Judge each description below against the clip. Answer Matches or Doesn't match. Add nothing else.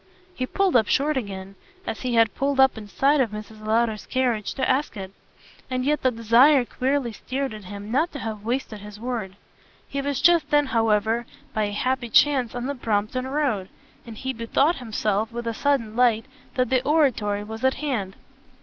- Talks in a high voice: Matches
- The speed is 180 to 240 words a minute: Matches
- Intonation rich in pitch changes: Doesn't match